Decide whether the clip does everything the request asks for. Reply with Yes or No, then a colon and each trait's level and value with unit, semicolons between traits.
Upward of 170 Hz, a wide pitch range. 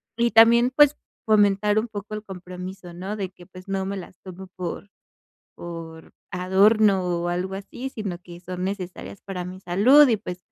No: high, 190 Hz; average, 2.8 semitones